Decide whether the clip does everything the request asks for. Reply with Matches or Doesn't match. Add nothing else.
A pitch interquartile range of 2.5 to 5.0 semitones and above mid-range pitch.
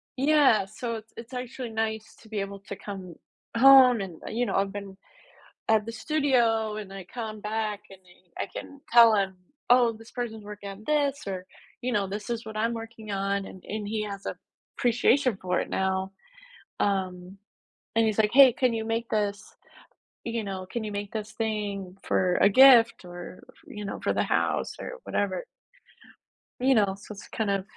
Matches